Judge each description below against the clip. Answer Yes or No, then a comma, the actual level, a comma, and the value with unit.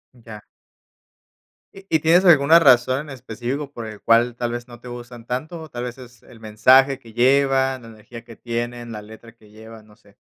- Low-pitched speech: Yes, low, 120 Hz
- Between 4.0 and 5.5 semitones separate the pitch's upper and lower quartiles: No, average, 2.7 semitones